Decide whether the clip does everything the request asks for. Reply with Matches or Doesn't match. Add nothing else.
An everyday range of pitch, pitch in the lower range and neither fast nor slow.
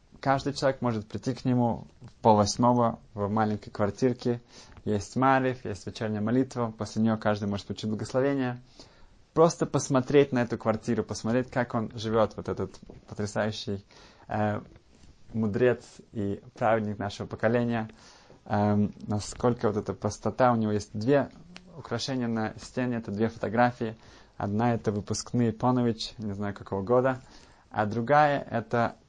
Matches